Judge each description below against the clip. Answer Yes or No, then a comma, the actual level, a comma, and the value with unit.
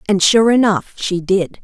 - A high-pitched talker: Yes, high, 195 Hz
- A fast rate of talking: No, average, 185 wpm